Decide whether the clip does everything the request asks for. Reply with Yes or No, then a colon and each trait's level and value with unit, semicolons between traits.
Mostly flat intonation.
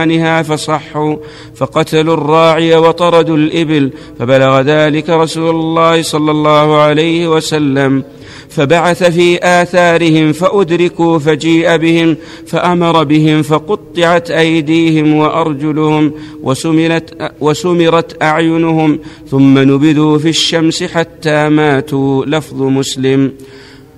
Yes: narrow, 1.4 semitones